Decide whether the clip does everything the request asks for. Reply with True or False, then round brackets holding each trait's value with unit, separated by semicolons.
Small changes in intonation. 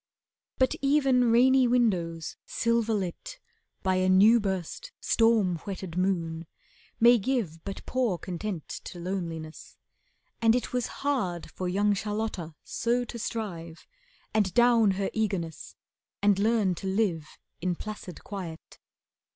False (4.7 semitones)